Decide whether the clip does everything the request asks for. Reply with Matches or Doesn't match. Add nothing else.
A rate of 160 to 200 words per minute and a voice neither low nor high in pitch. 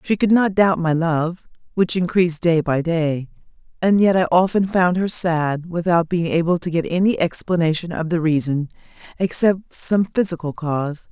Matches